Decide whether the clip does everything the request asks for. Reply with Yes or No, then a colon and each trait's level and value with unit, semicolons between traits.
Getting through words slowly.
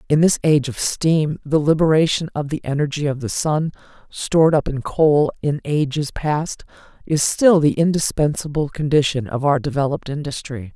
No: average, 160 wpm